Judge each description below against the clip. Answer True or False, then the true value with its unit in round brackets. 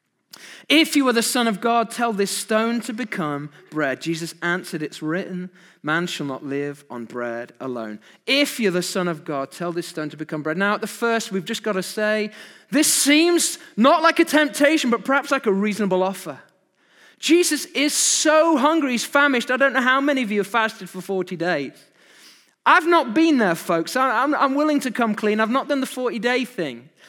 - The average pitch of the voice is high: True (220 Hz)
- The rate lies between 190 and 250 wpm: True (205 wpm)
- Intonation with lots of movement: True (8.0 semitones)